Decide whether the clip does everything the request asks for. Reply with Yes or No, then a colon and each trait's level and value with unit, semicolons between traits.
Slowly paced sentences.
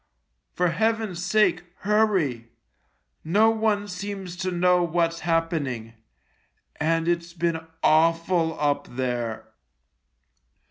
Yes: slow, 100 wpm